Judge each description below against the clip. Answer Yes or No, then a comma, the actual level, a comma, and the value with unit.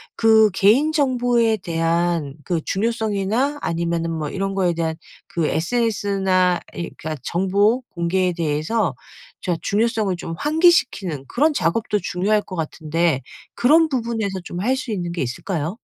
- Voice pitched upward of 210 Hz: No, high, 190 Hz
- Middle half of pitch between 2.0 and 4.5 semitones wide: No, average, 5.2 semitones